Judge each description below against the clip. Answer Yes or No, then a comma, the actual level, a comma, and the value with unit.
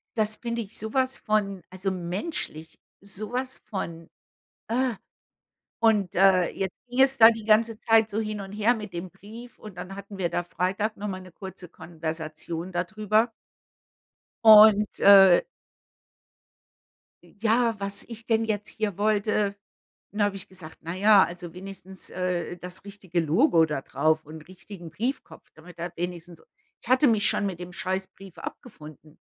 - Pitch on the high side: Yes, high, 195 Hz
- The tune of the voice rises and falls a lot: No, average, 3.6 semitones